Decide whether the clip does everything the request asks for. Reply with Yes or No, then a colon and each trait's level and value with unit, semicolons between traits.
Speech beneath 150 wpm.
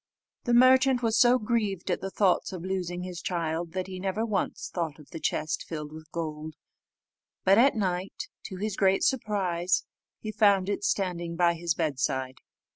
No: average, 175 wpm